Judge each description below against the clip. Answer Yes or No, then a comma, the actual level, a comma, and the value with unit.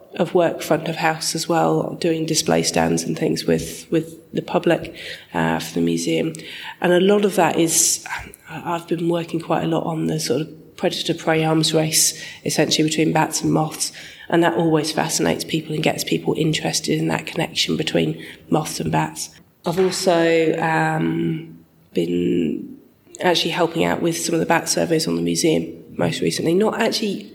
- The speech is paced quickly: No, average, 180 wpm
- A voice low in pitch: No, medium, 160 Hz